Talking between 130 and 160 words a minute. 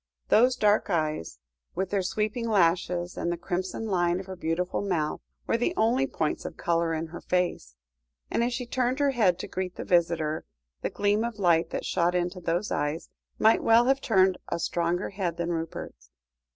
No: average, 190 wpm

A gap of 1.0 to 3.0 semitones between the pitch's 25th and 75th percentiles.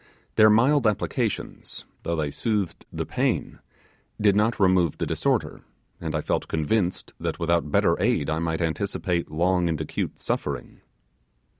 No: average, 4.6 semitones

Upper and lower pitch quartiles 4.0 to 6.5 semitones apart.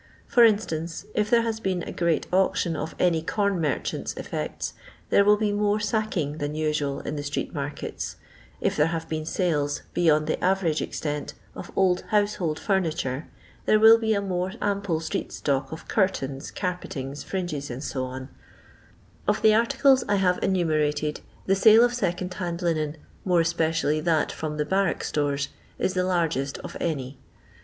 Yes: average, 4.7 semitones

